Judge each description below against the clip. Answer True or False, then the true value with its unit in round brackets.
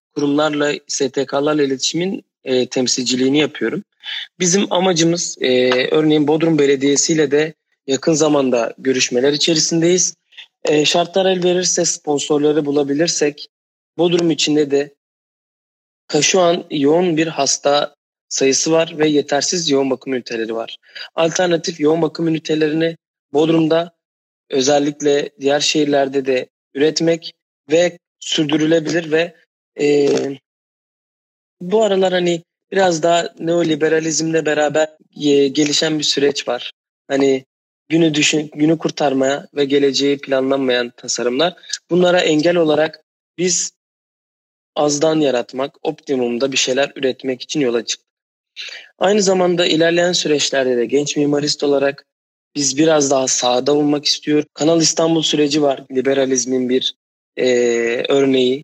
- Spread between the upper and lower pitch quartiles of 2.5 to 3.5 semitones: True (3.1 semitones)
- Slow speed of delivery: False (110 wpm)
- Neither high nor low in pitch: True (150 Hz)